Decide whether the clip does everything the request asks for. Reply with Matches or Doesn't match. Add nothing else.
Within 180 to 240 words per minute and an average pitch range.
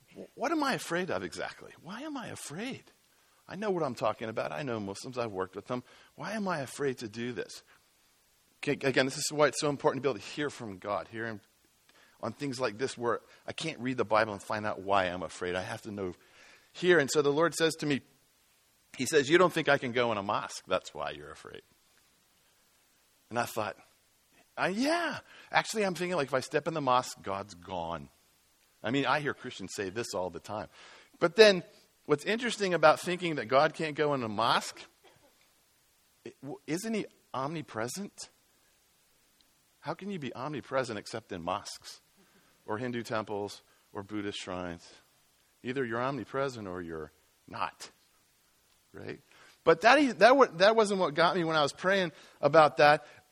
Doesn't match